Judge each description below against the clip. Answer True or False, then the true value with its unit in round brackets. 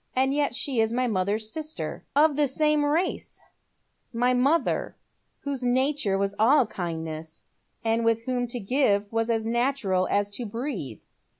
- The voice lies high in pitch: True (240 Hz)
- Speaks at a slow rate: False (155 wpm)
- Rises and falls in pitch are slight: False (5.3 semitones)